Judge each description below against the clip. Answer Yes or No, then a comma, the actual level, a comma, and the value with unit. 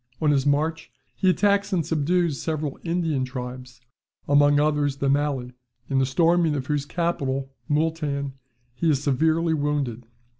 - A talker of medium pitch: Yes, medium, 145 Hz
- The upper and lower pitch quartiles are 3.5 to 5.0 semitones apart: No, average, 3.1 semitones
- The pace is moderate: Yes, average, 145 wpm